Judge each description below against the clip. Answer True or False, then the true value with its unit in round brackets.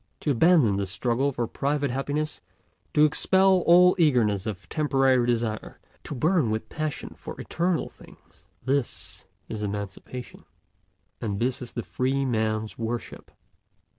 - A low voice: True (125 Hz)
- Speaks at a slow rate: True (130 wpm)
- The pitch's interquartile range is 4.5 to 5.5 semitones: True (5.2 semitones)